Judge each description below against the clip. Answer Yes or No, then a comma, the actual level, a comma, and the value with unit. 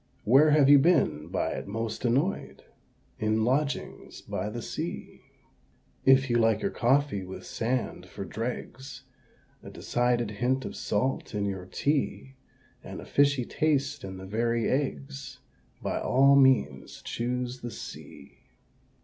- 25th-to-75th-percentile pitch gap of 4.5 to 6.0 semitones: No, average, 3.9 semitones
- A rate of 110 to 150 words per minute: Yes, average, 140 wpm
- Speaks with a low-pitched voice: Yes, low, 125 Hz